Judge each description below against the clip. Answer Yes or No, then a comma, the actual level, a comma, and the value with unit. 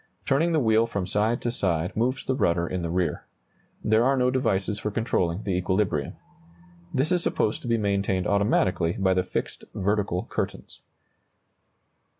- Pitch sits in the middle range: No, low, 100 Hz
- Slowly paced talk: No, average, 160 wpm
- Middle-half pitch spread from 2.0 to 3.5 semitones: No, average, 4.1 semitones